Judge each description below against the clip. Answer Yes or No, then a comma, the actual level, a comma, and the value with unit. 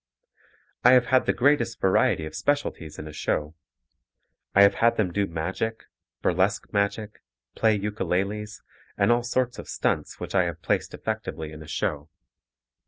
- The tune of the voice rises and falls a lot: Yes, wide, 6.0 semitones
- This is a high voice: No, low, 100 Hz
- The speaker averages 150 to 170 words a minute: Yes, average, 160 wpm